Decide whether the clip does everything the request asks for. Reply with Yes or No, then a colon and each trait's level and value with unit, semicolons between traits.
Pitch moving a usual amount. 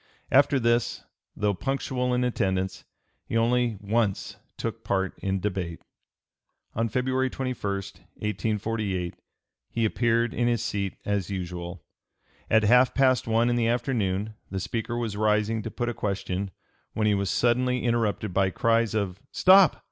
Yes: average, 3.4 semitones